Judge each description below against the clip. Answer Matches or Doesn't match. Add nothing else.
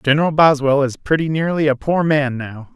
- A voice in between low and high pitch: Matches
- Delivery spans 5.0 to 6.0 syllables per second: Matches